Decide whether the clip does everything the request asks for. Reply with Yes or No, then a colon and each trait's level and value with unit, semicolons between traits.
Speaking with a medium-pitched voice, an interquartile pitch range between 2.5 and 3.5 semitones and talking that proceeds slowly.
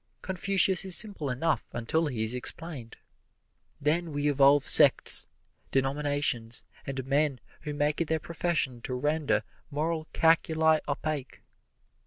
Yes: medium, 150 Hz; average, 3.2 semitones; slow, 125 wpm